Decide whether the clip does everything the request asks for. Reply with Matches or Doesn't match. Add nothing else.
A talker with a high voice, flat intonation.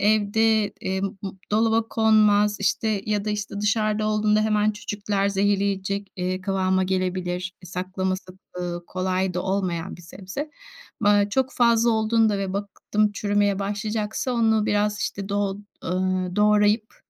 Matches